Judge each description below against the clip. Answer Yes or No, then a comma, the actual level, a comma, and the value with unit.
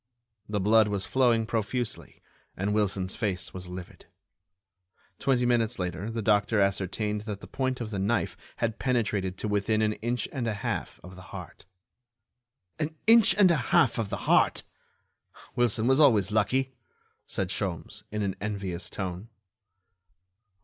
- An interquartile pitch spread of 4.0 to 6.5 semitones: No, average, 3.4 semitones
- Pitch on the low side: Yes, low, 105 Hz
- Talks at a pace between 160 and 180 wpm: No, average, 150 wpm